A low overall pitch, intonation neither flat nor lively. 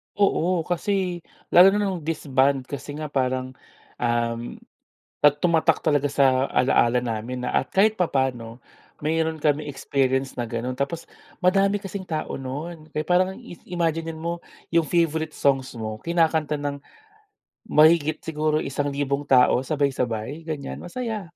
No: medium, 150 Hz; average, 4.2 semitones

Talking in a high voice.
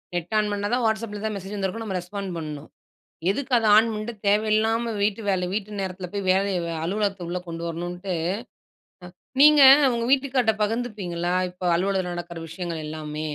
Yes: high, 195 Hz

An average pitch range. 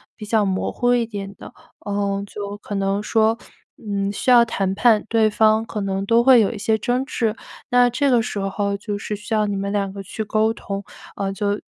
No: narrow, 2.2 semitones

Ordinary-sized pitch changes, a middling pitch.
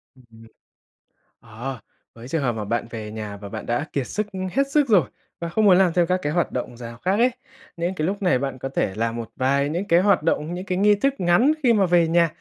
No: wide, 7.6 semitones; medium, 165 Hz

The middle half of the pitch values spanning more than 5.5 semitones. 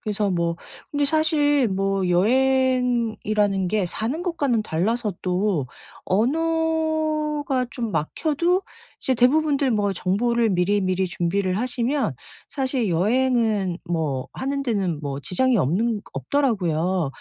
Yes: wide, 6.5 semitones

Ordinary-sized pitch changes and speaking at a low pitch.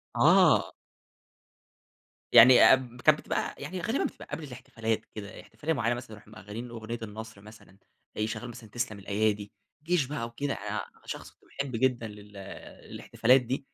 Yes: average, 3.4 semitones; low, 115 Hz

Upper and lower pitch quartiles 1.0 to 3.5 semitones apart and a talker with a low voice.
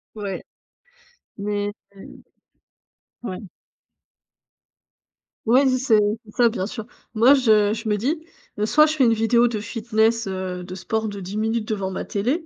No: average, 2.8 semitones; high, 220 Hz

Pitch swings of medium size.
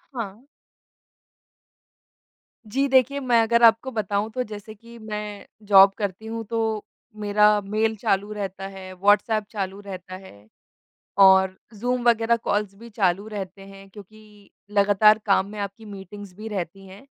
No: narrow, 2.2 semitones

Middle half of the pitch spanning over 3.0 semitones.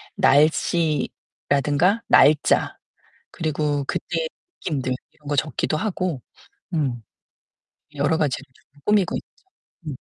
No: narrow, 2.5 semitones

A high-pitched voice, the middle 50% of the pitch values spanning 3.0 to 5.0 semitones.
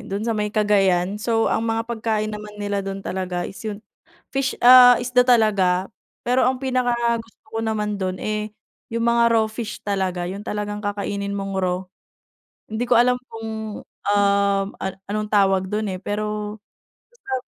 No: high, 210 Hz; narrow, 2.4 semitones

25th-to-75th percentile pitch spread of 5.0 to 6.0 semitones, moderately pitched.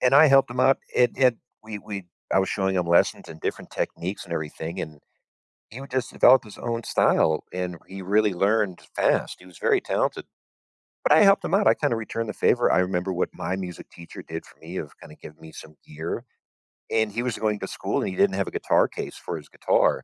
No: wide, 5.6 semitones; low, 100 Hz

